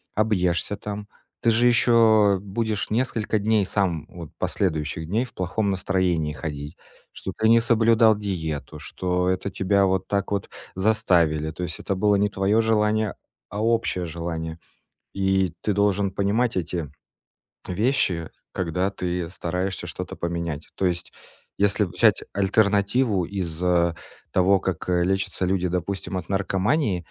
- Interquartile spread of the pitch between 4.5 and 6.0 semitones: No, average, 3.1 semitones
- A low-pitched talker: Yes, very low, 95 Hz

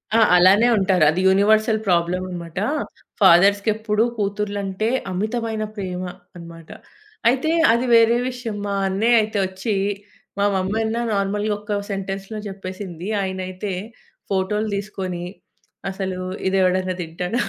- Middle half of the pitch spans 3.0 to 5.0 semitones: No, narrow, 2.6 semitones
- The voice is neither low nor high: No, high, 195 Hz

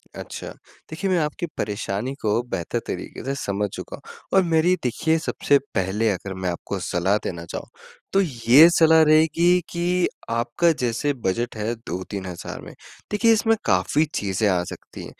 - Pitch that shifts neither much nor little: No, wide, 8.7 semitones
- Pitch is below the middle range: Yes, low, 120 Hz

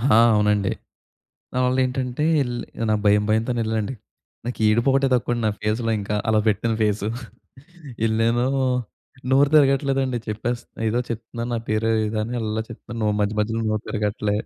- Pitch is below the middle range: Yes, low, 115 Hz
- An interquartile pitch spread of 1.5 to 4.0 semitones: Yes, narrow, 2.4 semitones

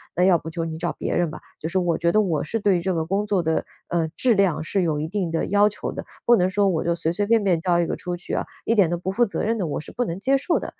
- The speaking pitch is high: No, medium, 180 Hz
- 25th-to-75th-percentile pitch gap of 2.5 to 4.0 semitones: Yes, average, 3.5 semitones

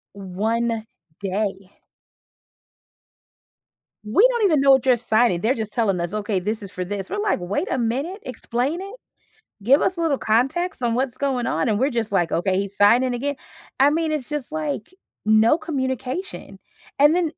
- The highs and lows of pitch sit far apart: Yes, wide, 5.7 semitones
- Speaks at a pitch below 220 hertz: No, high, 245 Hz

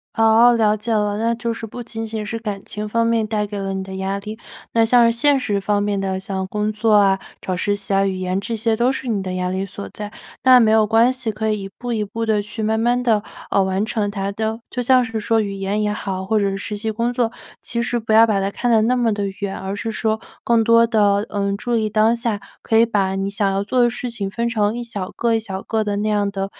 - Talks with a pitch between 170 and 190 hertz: No, high, 215 Hz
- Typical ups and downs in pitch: No, narrow, 2.3 semitones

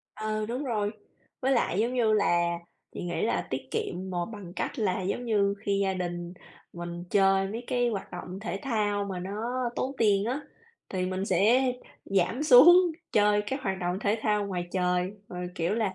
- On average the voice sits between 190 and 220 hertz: Yes, high, 200 Hz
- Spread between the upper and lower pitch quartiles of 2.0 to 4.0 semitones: Yes, average, 3.6 semitones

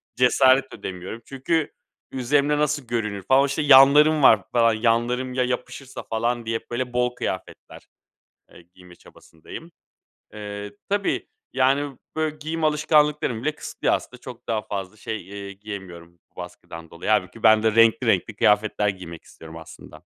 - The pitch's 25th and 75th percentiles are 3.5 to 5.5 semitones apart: Yes, average, 5.1 semitones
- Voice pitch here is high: No, low, 120 Hz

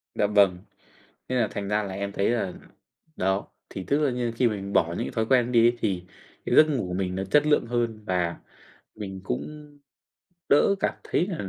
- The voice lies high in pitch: No, low, 105 Hz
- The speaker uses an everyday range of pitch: Yes, average, 4.4 semitones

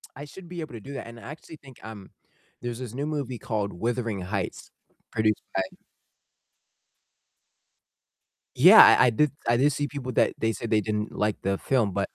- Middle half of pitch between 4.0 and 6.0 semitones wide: Yes, average, 4.6 semitones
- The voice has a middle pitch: No, low, 120 Hz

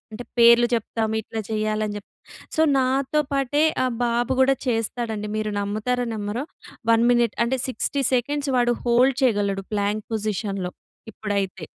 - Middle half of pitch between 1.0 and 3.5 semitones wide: Yes, average, 2.9 semitones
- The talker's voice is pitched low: No, high, 230 Hz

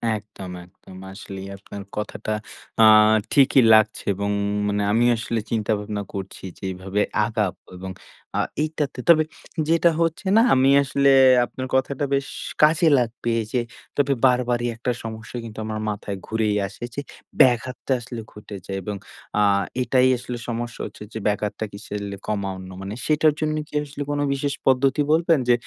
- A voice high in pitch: No, low, 115 Hz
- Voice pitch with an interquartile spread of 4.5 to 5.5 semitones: Yes, average, 4.8 semitones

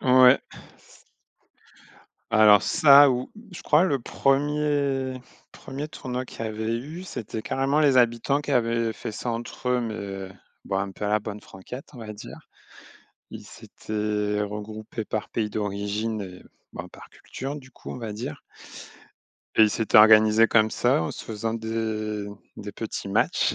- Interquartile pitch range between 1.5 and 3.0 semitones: No, average, 3.5 semitones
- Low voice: Yes, low, 115 Hz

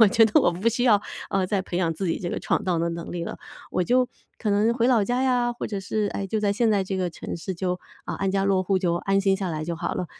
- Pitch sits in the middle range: No, high, 195 Hz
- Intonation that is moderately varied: Yes, average, 3.4 semitones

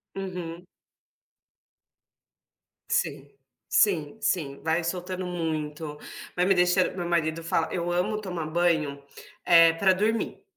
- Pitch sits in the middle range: Yes, medium, 175 Hz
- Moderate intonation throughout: No, narrow, 2.2 semitones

